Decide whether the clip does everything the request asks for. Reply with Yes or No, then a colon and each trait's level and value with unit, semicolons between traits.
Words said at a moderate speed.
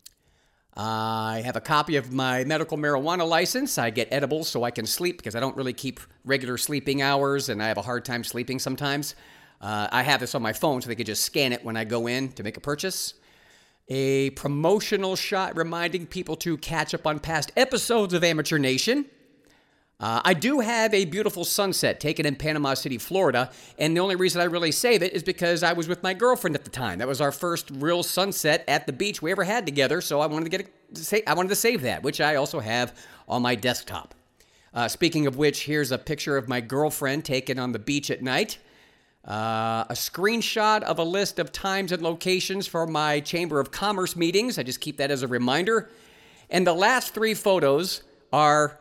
No: fast, 215 wpm